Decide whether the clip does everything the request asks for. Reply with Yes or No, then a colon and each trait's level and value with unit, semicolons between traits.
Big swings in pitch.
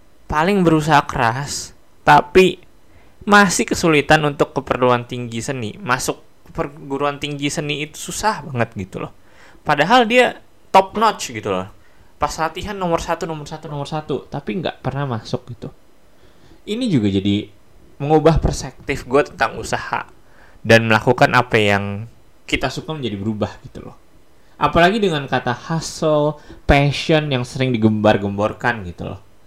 Yes: wide, 5.8 semitones